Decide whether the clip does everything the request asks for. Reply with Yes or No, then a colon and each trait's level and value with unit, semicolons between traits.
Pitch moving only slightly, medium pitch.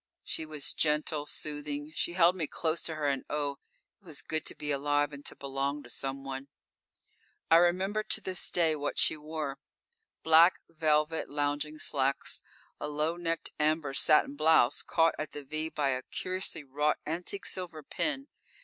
Yes: narrow, 2.1 semitones; medium, 150 Hz